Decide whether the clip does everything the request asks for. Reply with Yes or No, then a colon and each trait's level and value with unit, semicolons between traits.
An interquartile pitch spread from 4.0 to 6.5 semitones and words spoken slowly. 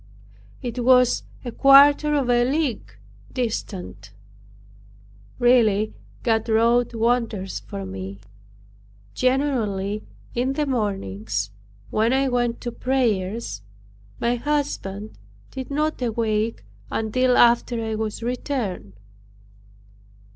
No: average, 3.5 semitones; slow, 95 wpm